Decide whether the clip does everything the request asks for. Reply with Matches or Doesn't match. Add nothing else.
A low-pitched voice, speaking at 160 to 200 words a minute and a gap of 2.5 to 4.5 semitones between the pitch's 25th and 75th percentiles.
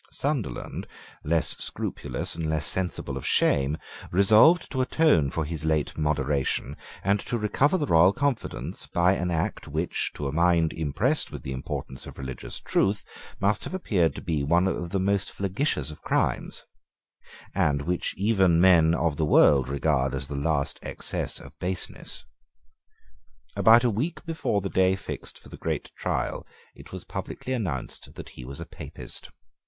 Doesn't match